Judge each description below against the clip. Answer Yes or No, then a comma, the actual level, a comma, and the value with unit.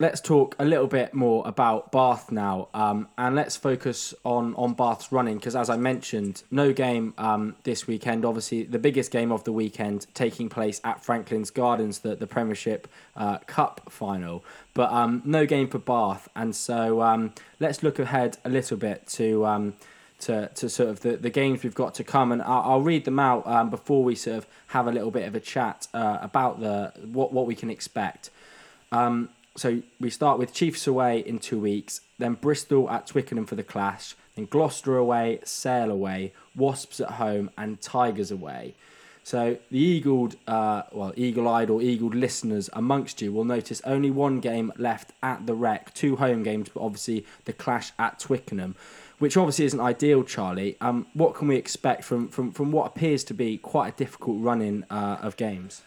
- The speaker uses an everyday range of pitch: Yes, average, 3.2 semitones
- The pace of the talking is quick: No, average, 195 wpm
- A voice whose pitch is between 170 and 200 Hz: No, low, 120 Hz